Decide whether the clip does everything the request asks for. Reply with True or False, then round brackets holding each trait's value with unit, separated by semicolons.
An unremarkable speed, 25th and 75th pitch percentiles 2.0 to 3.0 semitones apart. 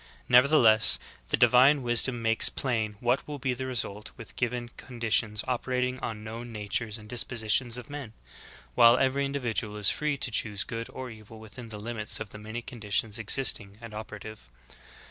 True (170 wpm; 2.7 semitones)